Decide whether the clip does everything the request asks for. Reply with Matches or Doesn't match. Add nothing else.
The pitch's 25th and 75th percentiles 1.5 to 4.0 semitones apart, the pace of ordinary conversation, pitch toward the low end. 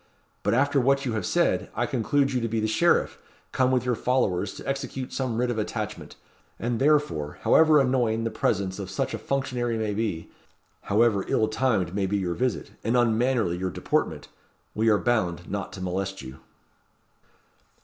Doesn't match